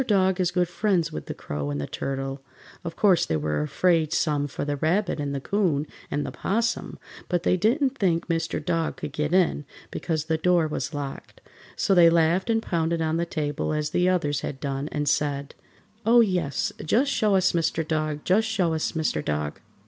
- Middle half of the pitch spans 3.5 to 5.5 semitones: Yes, average, 4.1 semitones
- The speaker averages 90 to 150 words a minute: No, average, 200 wpm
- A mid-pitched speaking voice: Yes, medium, 165 Hz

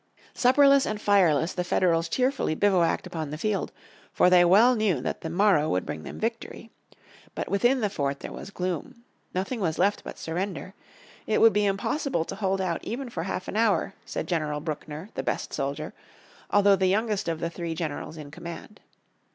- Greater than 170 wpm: Yes, average, 185 wpm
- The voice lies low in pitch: No, medium, 185 Hz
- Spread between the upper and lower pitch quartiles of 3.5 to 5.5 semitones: Yes, average, 4.5 semitones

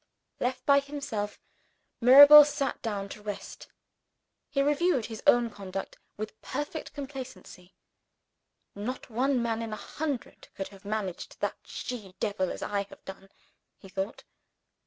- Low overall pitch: No, high, 230 Hz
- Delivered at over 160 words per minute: No, slow, 135 wpm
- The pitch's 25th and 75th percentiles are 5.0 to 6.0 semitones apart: Yes, wide, 5.4 semitones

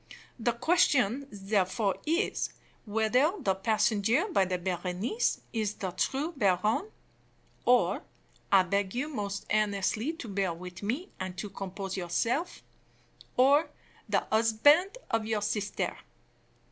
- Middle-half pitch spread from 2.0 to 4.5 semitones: No, average, 4.9 semitones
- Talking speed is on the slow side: Yes, slow, 120 wpm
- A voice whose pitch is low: No, high, 215 Hz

